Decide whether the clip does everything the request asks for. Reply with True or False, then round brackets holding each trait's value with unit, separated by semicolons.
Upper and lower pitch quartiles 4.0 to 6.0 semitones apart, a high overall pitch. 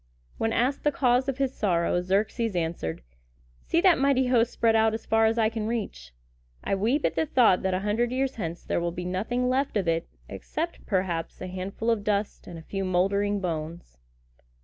True (5.2 semitones; 210 Hz)